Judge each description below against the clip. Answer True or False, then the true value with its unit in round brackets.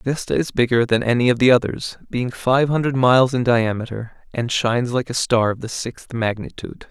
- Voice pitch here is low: True (120 Hz)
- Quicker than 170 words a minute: True (200 wpm)